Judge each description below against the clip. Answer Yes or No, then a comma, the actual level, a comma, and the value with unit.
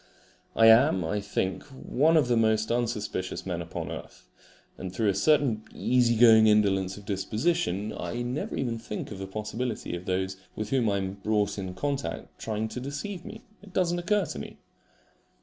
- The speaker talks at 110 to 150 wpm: No, average, 185 wpm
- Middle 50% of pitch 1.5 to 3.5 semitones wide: No, average, 4.6 semitones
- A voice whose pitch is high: No, low, 110 Hz